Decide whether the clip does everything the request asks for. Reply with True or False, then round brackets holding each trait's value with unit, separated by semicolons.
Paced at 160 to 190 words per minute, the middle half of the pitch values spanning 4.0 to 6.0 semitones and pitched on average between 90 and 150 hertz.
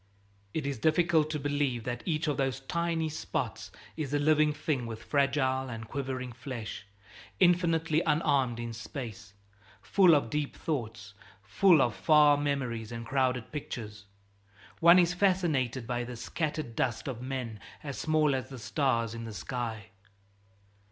False (150 wpm; 4.6 semitones; 135 Hz)